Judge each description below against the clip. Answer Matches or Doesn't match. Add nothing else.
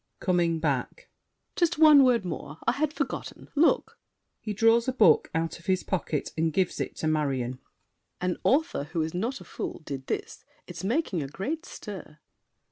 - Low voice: Doesn't match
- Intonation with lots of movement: Matches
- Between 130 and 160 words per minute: Doesn't match